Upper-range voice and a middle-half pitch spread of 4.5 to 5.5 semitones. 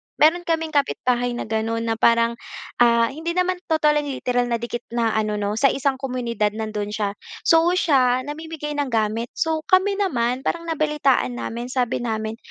Yes: high, 245 Hz; average, 4.8 semitones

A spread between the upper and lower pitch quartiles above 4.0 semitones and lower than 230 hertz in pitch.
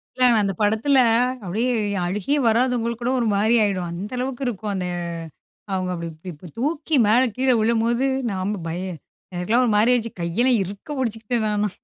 Yes: average, 4.4 semitones; high, 220 Hz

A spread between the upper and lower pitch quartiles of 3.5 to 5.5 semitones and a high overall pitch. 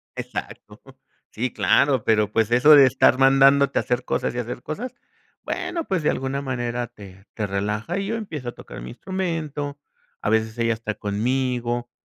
No: average, 4.3 semitones; low, 125 Hz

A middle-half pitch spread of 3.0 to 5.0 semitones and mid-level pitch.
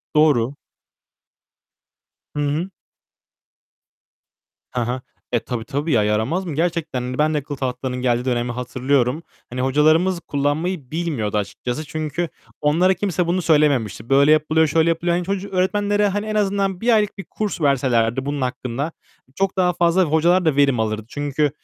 No: wide, 5.5 semitones; medium, 150 Hz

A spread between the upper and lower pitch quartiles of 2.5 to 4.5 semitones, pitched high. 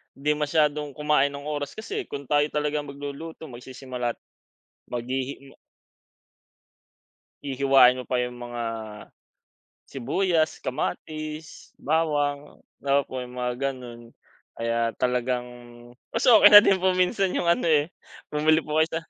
No: average, 3.5 semitones; medium, 145 Hz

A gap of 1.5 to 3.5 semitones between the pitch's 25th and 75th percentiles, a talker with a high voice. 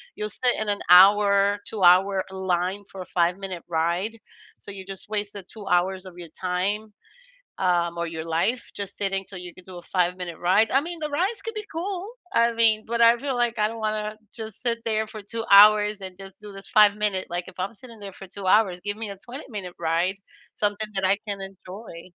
Yes: average, 2.9 semitones; high, 200 Hz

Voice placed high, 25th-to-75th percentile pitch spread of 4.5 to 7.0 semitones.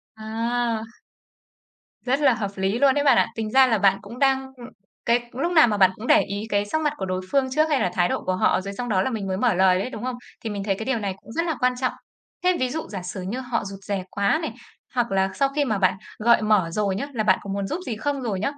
Yes: high, 225 Hz; average, 4.9 semitones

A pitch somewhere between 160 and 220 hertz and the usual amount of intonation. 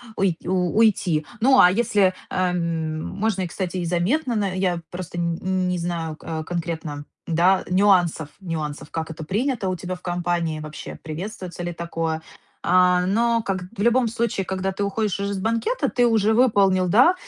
Yes: medium, 185 Hz; average, 3.2 semitones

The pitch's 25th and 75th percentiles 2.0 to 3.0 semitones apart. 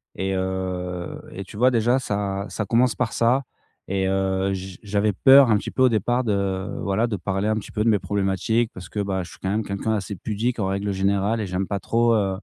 Yes: average, 2.7 semitones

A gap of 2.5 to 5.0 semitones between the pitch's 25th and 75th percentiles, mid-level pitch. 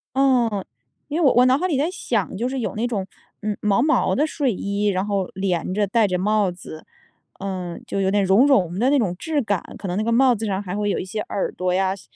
No: average, 4.7 semitones; high, 205 Hz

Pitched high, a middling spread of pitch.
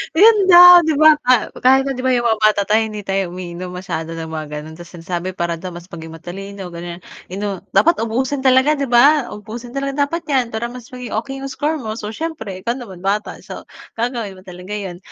No: high, 215 Hz; wide, 6.5 semitones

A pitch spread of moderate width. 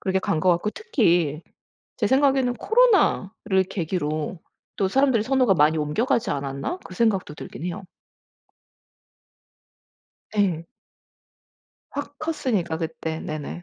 No: wide, 7.9 semitones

